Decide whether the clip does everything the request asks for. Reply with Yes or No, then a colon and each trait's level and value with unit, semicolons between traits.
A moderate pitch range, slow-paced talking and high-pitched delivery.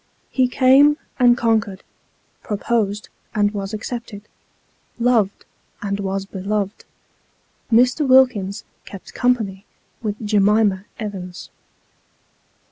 Yes: average, 3.5 semitones; slow, 105 wpm; high, 210 Hz